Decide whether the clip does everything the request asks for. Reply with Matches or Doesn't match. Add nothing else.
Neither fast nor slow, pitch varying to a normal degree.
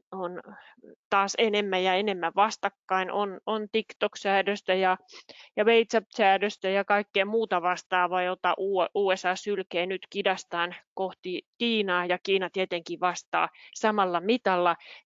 Doesn't match